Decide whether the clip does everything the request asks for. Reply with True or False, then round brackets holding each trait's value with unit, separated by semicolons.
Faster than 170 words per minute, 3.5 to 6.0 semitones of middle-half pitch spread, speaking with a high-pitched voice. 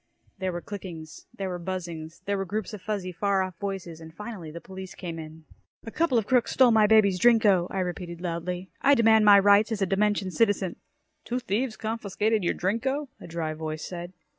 True (200 wpm; 3.8 semitones; 195 Hz)